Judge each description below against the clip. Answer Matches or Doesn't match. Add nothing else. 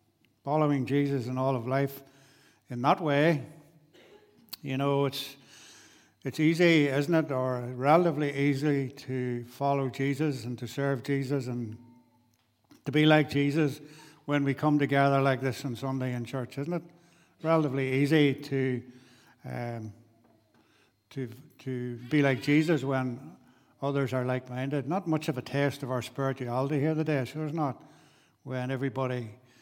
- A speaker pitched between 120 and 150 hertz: Matches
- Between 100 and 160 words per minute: Matches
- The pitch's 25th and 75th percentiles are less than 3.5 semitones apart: Matches